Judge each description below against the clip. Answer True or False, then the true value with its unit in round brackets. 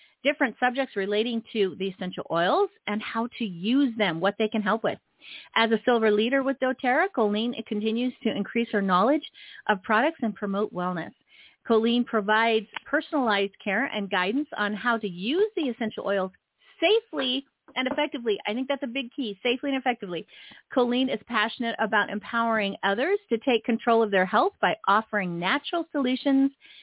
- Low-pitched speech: False (230 Hz)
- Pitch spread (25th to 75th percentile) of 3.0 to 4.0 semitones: False (4.7 semitones)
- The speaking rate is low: False (170 wpm)